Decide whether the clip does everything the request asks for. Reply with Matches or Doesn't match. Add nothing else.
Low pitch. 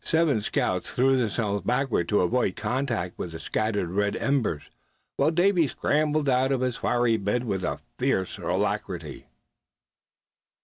Matches